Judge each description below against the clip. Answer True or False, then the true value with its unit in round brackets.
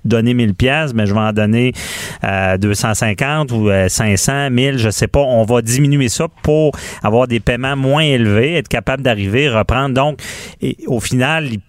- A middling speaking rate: True (180 wpm)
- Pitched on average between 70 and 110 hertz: False (120 Hz)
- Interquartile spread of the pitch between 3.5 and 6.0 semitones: True (4.2 semitones)